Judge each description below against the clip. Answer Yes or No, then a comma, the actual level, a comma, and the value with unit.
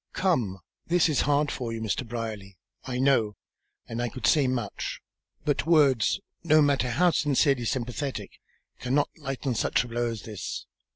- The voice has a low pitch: Yes, low, 130 Hz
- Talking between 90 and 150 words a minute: No, average, 160 wpm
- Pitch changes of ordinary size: Yes, average, 3.9 semitones